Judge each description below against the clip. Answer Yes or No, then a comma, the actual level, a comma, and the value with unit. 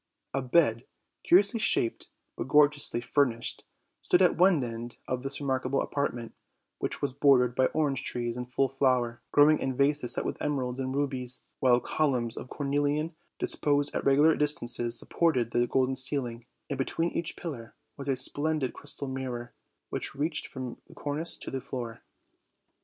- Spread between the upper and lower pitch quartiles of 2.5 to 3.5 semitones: Yes, average, 2.9 semitones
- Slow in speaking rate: No, average, 160 wpm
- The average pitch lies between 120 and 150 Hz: Yes, low, 135 Hz